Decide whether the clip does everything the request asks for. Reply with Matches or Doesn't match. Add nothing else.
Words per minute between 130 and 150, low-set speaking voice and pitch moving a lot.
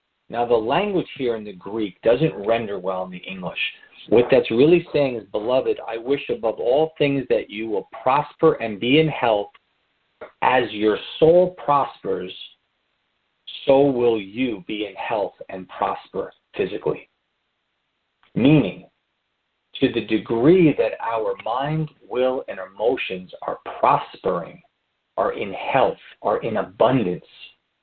Matches